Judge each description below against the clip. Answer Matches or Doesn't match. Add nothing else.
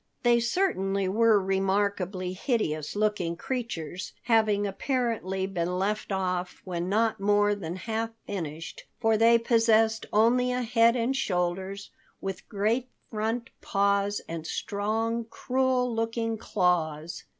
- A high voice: Matches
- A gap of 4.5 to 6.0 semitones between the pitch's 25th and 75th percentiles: Doesn't match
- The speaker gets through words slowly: Matches